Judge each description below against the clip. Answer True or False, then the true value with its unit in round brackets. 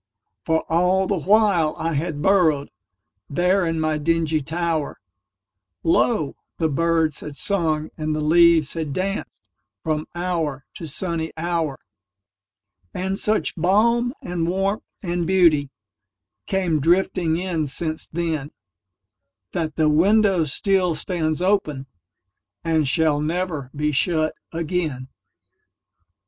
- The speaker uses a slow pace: True (100 wpm)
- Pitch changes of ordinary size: True (4.6 semitones)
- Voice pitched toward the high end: False (160 Hz)